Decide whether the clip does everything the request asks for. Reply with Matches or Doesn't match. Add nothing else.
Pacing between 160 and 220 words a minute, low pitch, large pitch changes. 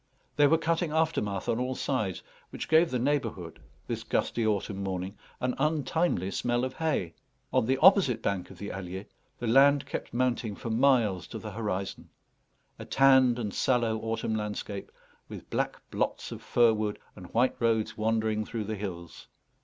Doesn't match